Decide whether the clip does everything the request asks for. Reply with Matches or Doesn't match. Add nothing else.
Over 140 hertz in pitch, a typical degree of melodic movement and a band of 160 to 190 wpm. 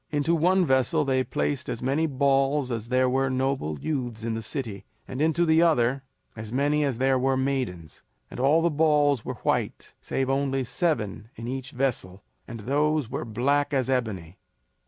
Doesn't match